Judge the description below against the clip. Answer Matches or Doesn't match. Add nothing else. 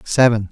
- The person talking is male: Matches